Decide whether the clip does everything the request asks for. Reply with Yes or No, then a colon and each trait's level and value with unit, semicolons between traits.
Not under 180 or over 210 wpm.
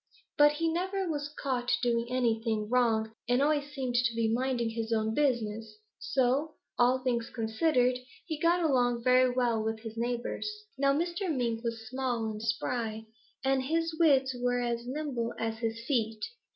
No: average, 165 wpm